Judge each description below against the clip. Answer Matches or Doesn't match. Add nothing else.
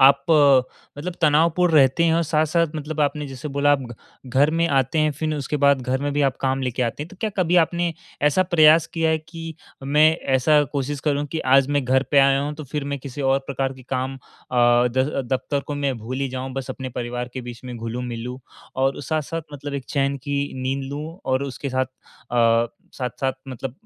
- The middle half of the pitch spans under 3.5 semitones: Matches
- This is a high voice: Doesn't match